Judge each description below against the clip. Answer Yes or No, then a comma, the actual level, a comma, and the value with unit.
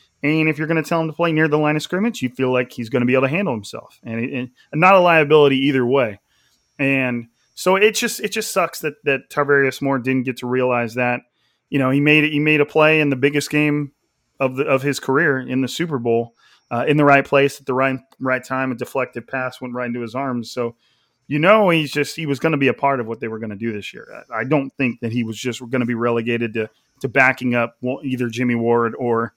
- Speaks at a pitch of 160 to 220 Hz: No, low, 135 Hz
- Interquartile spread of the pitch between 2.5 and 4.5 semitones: Yes, average, 3.5 semitones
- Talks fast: Yes, fast, 265 wpm